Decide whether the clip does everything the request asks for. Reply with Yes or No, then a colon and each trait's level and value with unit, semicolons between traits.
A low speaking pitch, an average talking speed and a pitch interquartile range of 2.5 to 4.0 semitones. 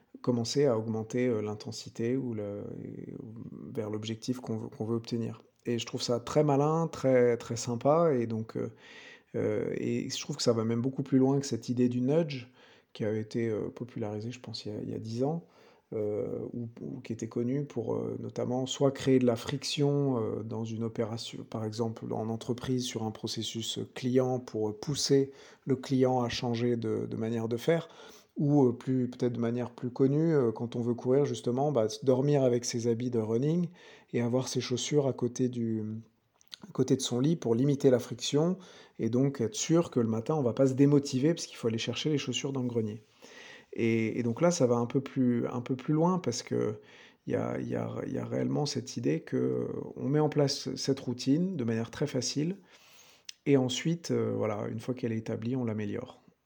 Yes: low, 125 Hz; average, 200 wpm; average, 3.1 semitones